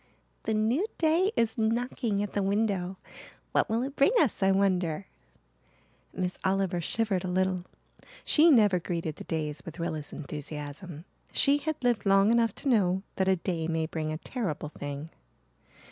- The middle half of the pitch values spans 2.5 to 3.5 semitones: No, average, 5.3 semitones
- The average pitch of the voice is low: No, high, 190 Hz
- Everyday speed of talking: Yes, average, 160 wpm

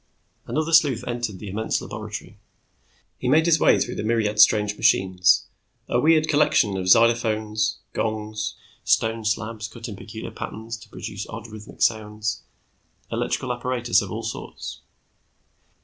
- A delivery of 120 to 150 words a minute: Yes, average, 140 wpm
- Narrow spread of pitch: Yes, narrow, 2.1 semitones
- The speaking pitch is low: Yes, low, 110 Hz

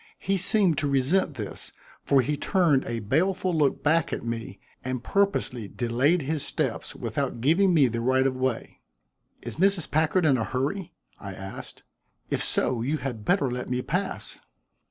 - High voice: No, medium, 140 Hz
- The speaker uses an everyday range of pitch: No, wide, 5.7 semitones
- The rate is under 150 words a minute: No, average, 170 wpm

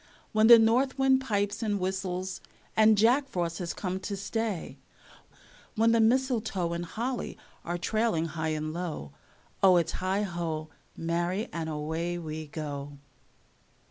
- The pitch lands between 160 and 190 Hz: Yes, medium, 185 Hz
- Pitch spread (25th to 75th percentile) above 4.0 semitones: Yes, average, 4.9 semitones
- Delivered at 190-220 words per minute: No, average, 140 wpm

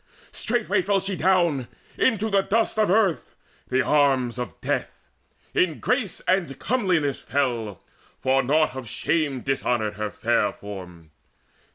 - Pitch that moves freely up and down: Yes, wide, 7.7 semitones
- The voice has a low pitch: No, medium, 145 Hz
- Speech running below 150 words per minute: Yes, slow, 135 wpm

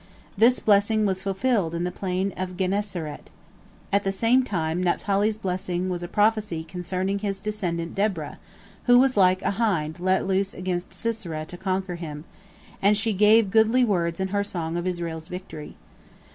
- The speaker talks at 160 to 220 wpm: Yes, average, 165 wpm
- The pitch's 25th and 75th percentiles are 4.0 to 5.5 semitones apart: No, average, 3.0 semitones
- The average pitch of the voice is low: No, high, 190 Hz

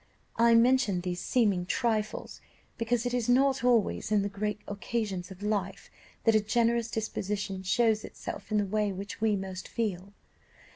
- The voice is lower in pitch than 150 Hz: No, high, 210 Hz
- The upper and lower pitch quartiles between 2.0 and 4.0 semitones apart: Yes, average, 2.9 semitones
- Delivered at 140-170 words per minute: Yes, average, 160 wpm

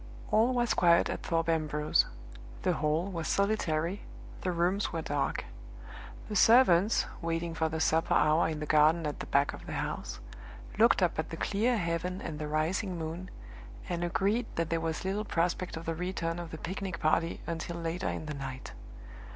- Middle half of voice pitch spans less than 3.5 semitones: Yes, average, 2.7 semitones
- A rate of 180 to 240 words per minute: Yes, average, 185 wpm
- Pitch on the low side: No, medium, 170 Hz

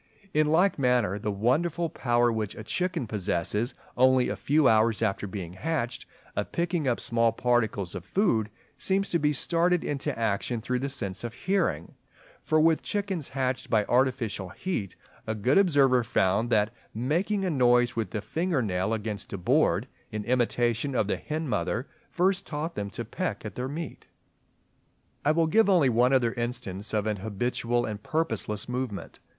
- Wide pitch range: Yes, wide, 6.3 semitones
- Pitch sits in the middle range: No, low, 125 Hz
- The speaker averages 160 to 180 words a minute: Yes, average, 170 wpm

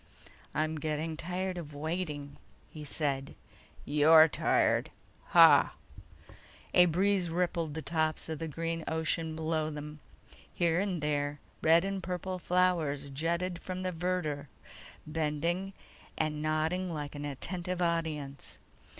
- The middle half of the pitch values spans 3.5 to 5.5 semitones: No, average, 2.9 semitones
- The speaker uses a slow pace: Yes, slow, 125 wpm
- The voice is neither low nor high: Yes, medium, 160 Hz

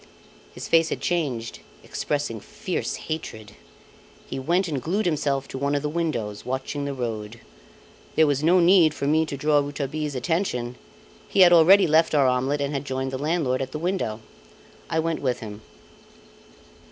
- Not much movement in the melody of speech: No, average, 3.7 semitones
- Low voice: No, medium, 145 Hz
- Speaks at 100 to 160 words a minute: No, average, 170 wpm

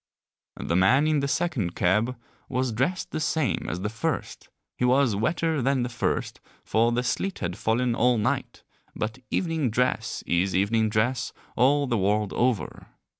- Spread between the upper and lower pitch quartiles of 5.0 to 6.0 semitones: No, average, 4.2 semitones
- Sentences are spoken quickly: No, average, 165 wpm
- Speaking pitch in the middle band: No, low, 120 Hz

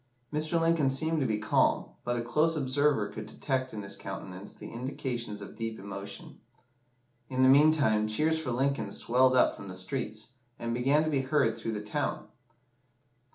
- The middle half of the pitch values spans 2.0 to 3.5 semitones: No, average, 5.1 semitones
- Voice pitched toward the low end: Yes, low, 130 Hz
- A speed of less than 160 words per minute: No, average, 175 wpm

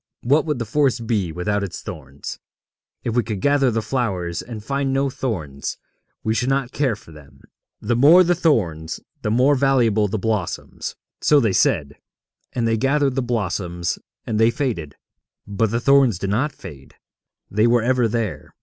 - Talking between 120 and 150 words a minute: No, average, 175 wpm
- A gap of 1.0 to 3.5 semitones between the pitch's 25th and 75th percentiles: No, average, 5.2 semitones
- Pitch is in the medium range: No, low, 115 Hz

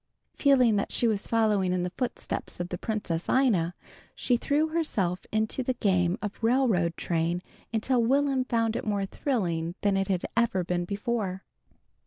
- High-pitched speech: Yes, high, 210 Hz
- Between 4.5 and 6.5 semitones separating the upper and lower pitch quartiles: Yes, average, 5.1 semitones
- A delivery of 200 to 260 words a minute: No, average, 170 wpm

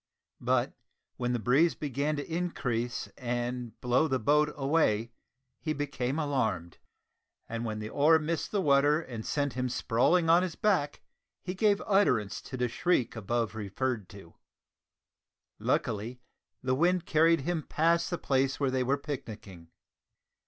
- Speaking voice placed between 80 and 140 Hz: Yes, low, 135 Hz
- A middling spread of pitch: Yes, average, 5.0 semitones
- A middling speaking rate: Yes, average, 145 wpm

